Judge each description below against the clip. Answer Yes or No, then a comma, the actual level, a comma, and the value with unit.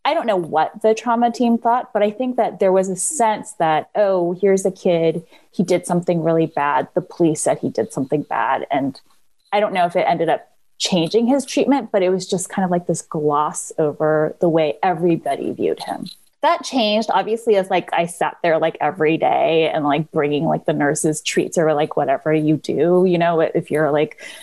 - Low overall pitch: No, medium, 175 Hz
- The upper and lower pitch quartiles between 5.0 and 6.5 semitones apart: Yes, average, 5.3 semitones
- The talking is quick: Yes, fast, 215 wpm